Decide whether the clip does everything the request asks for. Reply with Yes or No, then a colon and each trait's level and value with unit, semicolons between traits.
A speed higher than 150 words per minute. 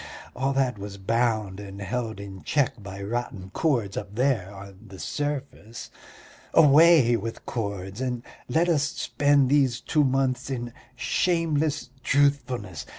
No: slow, 135 wpm